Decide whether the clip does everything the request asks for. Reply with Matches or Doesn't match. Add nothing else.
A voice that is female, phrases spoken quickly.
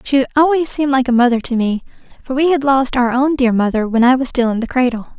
Matches